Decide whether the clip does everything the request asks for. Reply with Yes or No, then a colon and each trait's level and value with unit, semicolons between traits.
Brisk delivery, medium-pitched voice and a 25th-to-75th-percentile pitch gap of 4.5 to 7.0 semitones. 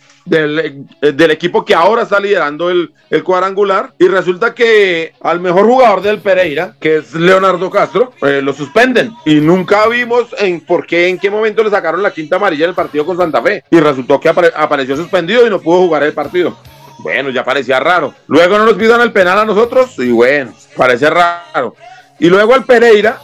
Yes: fast, 195 wpm; medium, 180 Hz; average, 5.3 semitones